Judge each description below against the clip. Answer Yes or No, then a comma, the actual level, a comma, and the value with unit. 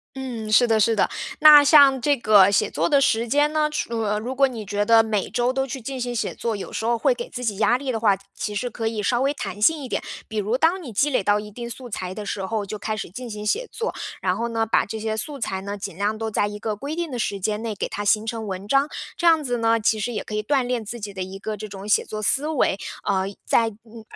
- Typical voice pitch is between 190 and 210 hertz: No, high, 225 Hz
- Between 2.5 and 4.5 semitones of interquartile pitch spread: Yes, average, 3.8 semitones